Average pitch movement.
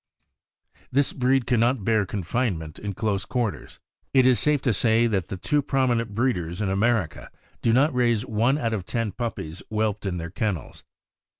Yes: average, 4.1 semitones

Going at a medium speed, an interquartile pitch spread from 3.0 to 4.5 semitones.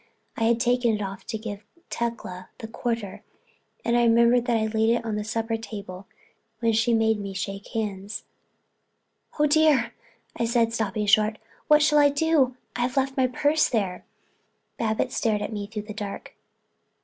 No: average, 165 wpm; narrow, 2.5 semitones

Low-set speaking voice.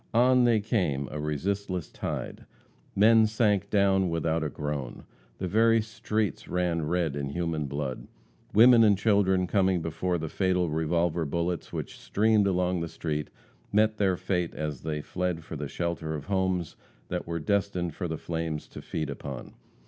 Yes: very low, 90 Hz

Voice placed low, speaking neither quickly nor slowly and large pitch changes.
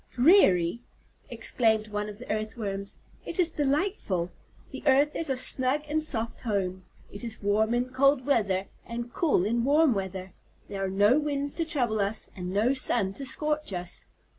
No: high, 230 Hz; average, 170 wpm; wide, 5.8 semitones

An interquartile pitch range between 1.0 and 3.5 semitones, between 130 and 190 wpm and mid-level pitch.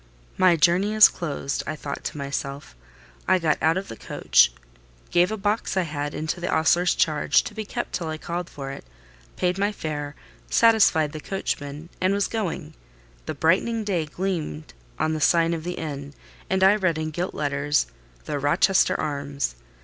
No: average, 4.3 semitones; average, 180 wpm; medium, 160 Hz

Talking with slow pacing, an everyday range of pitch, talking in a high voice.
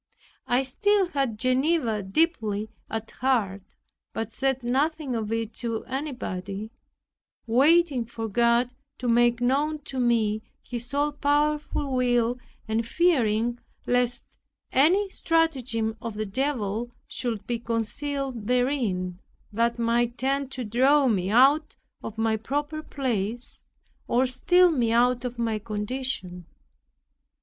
Yes: slow, 125 wpm; average, 3.6 semitones; high, 245 Hz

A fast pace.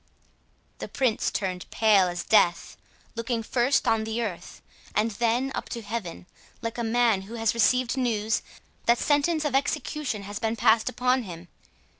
No: average, 170 wpm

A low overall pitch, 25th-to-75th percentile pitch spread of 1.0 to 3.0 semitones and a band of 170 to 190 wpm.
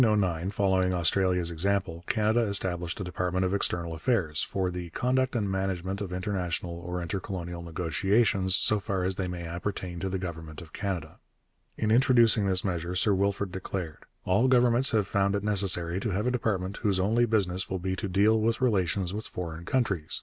Yes: very low, 95 Hz; average, 2.7 semitones; average, 185 wpm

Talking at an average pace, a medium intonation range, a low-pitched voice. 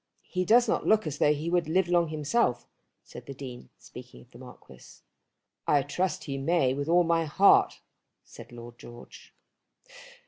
No: average, 170 wpm; average, 4.4 semitones; medium, 155 Hz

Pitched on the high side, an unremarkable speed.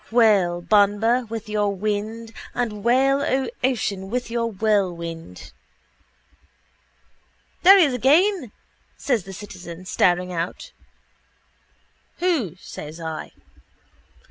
No: high, 215 Hz; slow, 100 wpm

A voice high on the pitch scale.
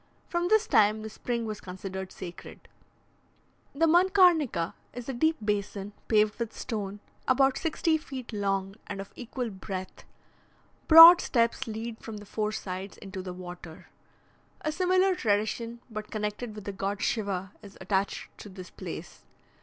Yes: high, 215 Hz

